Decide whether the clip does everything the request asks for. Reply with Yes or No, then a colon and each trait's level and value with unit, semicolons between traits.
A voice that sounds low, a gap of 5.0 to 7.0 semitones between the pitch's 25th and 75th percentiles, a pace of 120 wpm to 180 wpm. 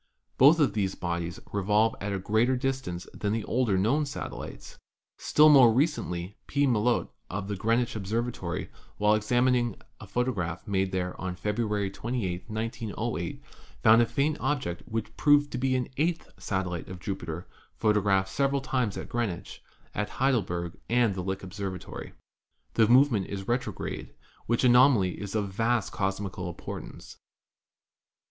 No: low, 110 Hz; average, 4.5 semitones; average, 145 wpm